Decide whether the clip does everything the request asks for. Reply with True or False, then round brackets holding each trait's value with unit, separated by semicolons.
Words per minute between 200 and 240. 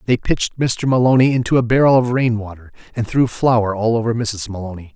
True (205 wpm)